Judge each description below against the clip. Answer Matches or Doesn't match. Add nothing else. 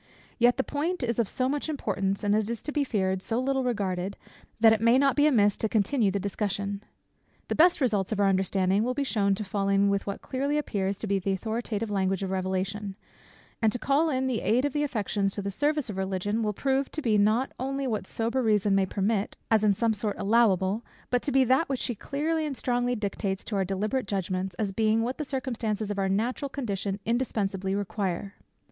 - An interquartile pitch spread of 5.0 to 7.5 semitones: Doesn't match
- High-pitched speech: Matches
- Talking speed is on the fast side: Matches